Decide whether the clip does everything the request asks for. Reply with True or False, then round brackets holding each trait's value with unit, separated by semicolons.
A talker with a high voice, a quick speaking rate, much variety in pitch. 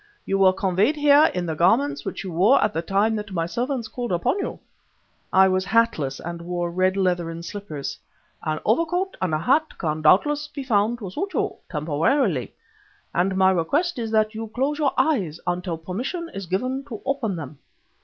False (195 Hz; 185 wpm; 6.9 semitones)